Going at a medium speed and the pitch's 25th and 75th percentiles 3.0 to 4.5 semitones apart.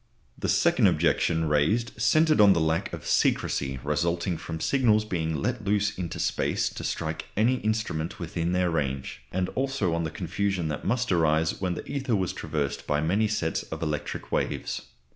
No: average, 175 wpm; average, 5.2 semitones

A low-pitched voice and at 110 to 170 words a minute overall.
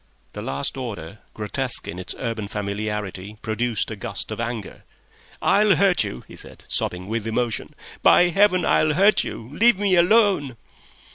Yes: low, 115 Hz; average, 155 wpm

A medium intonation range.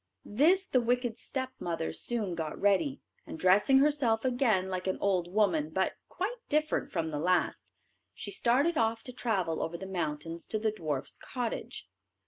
No: wide, 6.3 semitones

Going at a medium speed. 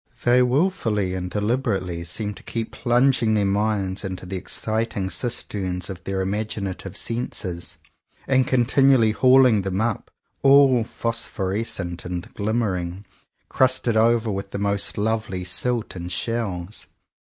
No: slow, 130 wpm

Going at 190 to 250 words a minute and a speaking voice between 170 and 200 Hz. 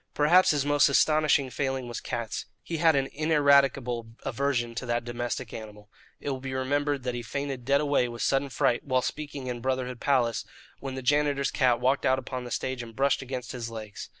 No: average, 200 wpm; low, 130 Hz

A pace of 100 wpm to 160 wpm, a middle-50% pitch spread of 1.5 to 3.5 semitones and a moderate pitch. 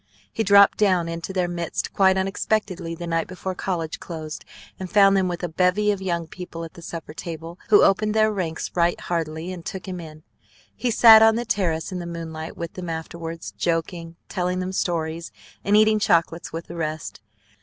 No: average, 195 wpm; narrow, 2.5 semitones; medium, 175 Hz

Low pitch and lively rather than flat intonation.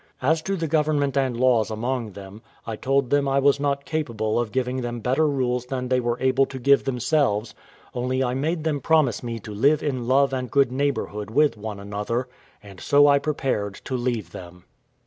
No: low, 130 Hz; average, 3.4 semitones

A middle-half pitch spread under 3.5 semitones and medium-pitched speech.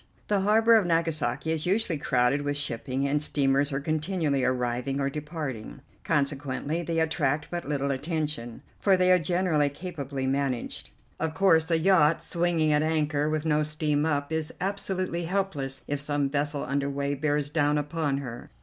Yes: average, 2.8 semitones; medium, 150 Hz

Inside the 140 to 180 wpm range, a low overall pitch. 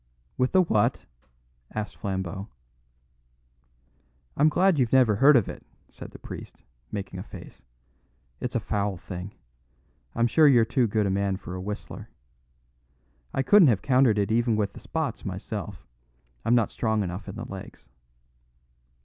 Yes: average, 155 wpm; low, 110 Hz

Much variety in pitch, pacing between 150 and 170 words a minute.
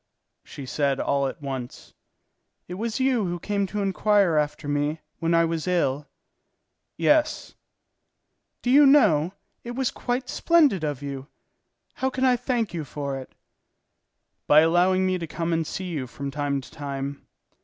Yes: wide, 6.6 semitones; average, 165 wpm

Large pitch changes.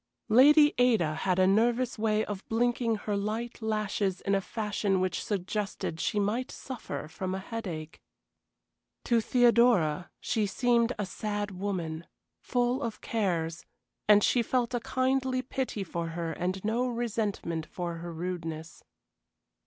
No: average, 4.6 semitones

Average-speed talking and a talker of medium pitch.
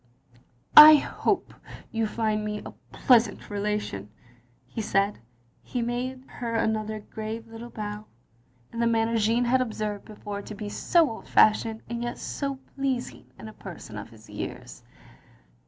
No: average, 170 wpm; high, 220 Hz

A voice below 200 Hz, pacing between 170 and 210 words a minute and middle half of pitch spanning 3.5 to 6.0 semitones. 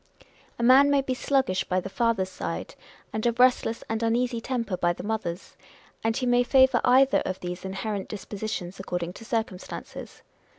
No: high, 225 Hz; average, 175 wpm; average, 4.7 semitones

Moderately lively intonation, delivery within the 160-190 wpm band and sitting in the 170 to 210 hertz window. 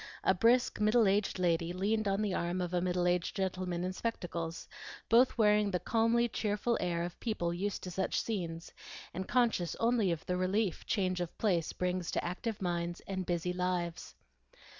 Yes: average, 3.3 semitones; average, 180 wpm; medium, 185 Hz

